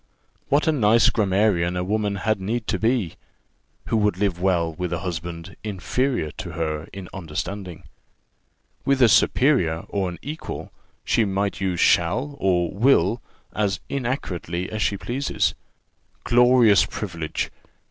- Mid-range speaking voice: No, low, 100 Hz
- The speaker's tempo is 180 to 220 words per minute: No, slow, 135 wpm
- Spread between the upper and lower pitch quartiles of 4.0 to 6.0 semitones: Yes, average, 4.6 semitones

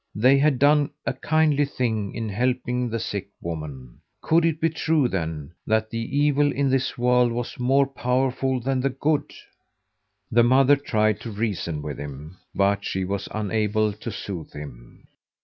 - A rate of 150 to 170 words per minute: Yes, average, 165 wpm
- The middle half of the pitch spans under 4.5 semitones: No, wide, 5.4 semitones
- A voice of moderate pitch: No, low, 120 Hz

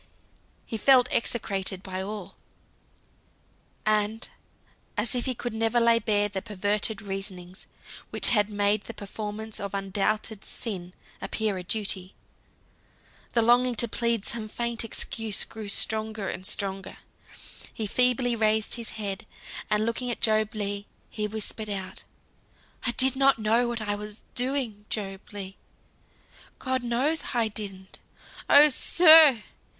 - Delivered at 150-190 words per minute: No, slow, 135 wpm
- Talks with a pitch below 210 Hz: No, high, 215 Hz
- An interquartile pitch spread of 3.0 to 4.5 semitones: No, narrow, 2.6 semitones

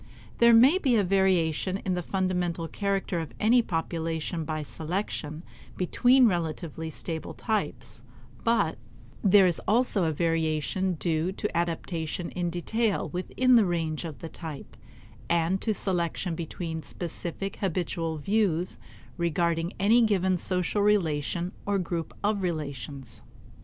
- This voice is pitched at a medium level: Yes, medium, 175 Hz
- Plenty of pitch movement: No, average, 3.3 semitones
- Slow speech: Yes, slow, 130 wpm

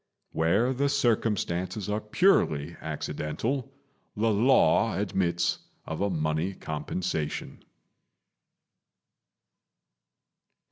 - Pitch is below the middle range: Yes, very low, 95 Hz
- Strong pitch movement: Yes, wide, 5.9 semitones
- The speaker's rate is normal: No, slow, 75 wpm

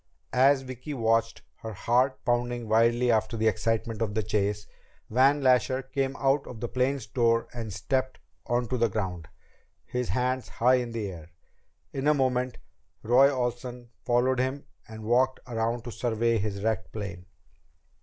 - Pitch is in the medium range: No, low, 120 Hz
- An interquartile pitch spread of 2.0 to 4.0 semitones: Yes, narrow, 2.6 semitones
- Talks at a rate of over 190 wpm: No, average, 155 wpm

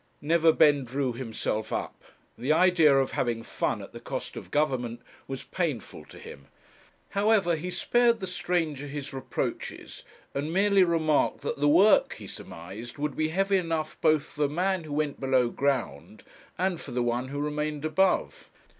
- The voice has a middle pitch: Yes, medium, 150 Hz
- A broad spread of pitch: No, average, 4.8 semitones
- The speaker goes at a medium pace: Yes, average, 165 wpm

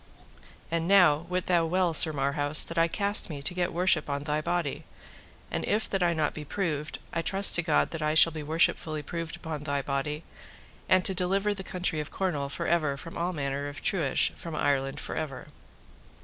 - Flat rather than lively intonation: No, average, 3.3 semitones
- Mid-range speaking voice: Yes, medium, 160 Hz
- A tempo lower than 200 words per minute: No, fast, 205 wpm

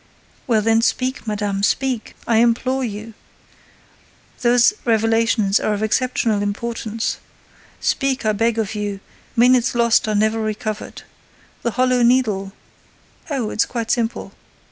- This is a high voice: Yes, high, 225 Hz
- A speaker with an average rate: No, slow, 125 wpm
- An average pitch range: No, narrow, 2.2 semitones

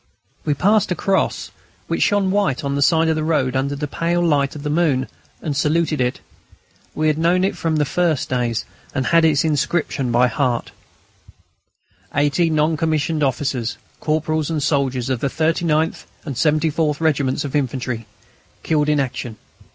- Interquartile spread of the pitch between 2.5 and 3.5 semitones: Yes, average, 3.2 semitones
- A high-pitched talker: No, medium, 150 Hz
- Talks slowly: No, average, 165 wpm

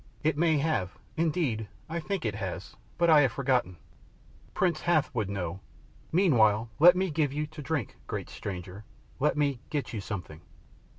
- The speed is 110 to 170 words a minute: Yes, average, 165 wpm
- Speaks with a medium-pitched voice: Yes, medium, 145 Hz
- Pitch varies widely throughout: Yes, wide, 7.0 semitones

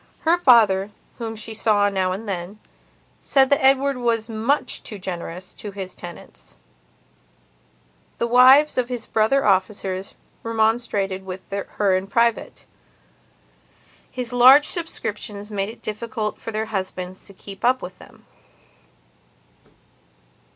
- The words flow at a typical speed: No, slow, 125 wpm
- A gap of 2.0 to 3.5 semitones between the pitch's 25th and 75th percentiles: No, average, 3.9 semitones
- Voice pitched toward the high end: Yes, high, 215 Hz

